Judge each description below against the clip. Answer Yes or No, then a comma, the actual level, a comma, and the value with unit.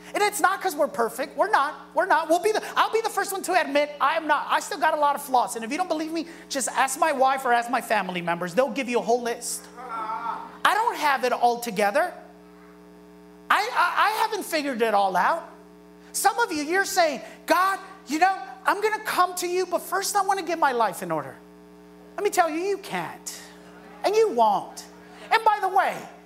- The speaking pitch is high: Yes, very high, 295 Hz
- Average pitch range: No, wide, 8.6 semitones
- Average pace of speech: No, fast, 235 wpm